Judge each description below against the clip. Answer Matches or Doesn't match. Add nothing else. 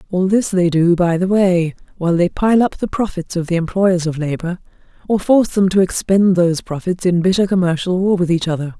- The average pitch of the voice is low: Doesn't match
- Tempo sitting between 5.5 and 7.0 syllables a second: Matches